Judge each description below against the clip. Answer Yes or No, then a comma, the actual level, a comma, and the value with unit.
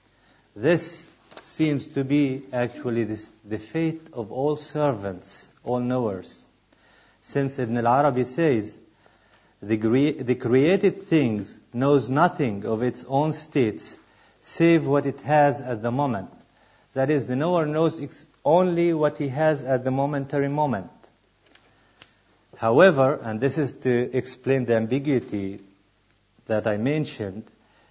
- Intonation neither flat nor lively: Yes, average, 4.7 semitones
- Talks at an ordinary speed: No, slow, 125 wpm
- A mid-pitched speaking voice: No, low, 130 Hz